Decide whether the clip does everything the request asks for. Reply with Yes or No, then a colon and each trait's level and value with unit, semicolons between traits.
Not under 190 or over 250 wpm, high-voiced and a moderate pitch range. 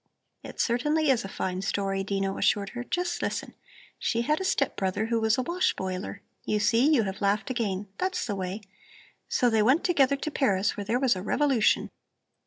No: average, 195 wpm; high, 225 Hz; wide, 5.8 semitones